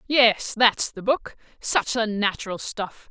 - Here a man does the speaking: No, female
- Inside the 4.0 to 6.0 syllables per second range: No, 3.8 syllables/s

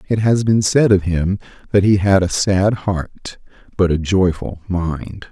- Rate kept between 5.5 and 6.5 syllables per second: No, 3.9 syllables/s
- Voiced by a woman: No, male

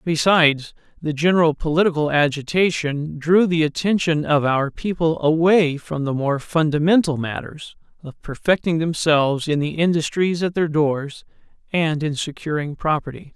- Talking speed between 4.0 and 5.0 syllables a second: Yes, 4.7 syllables/s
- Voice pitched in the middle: Yes, medium, 155 Hz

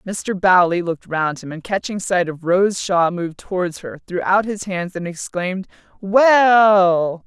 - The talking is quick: No, average, 175 wpm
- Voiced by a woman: Yes, female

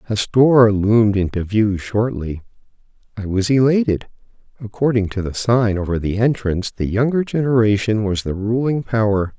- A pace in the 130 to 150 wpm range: Yes, average, 145 wpm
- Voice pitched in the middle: No, low, 110 Hz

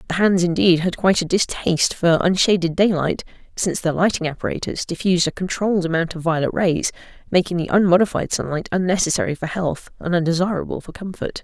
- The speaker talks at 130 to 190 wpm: Yes, average, 170 wpm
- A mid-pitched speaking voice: Yes, medium, 175 Hz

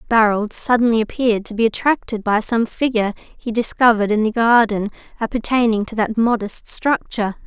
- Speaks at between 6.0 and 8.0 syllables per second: No, 5.6 syllables/s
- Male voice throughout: No, female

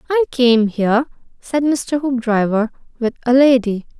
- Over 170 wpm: No, slow, 135 wpm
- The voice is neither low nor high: No, very high, 250 Hz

